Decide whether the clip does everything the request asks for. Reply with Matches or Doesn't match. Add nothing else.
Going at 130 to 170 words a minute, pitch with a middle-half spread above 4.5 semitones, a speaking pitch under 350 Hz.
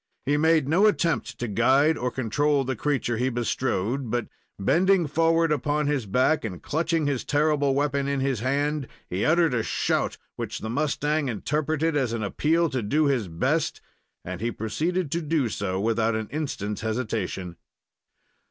Matches